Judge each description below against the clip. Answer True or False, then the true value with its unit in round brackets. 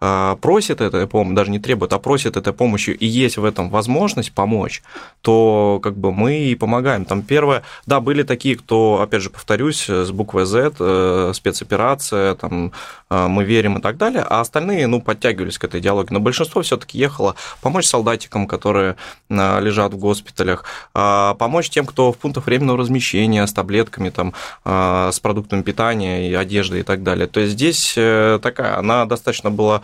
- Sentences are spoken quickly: True (170 wpm)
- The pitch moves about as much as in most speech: True (3.8 semitones)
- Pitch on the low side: True (105 Hz)